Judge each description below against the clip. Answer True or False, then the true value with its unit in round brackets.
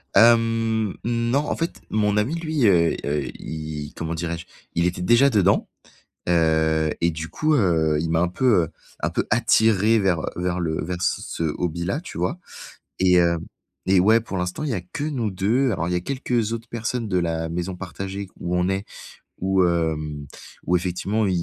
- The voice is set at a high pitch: False (95 Hz)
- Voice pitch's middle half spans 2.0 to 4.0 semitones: False (5.1 semitones)